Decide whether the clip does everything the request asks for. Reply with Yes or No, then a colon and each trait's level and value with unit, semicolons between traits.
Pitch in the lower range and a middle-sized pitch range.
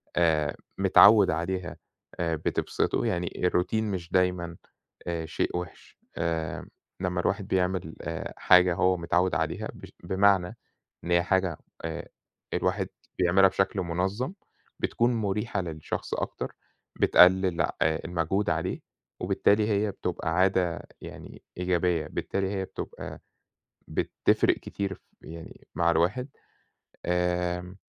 No: very low, 90 Hz; narrow, 2.1 semitones